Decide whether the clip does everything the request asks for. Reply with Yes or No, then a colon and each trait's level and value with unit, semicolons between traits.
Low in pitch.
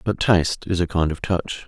Yes: very low, 90 Hz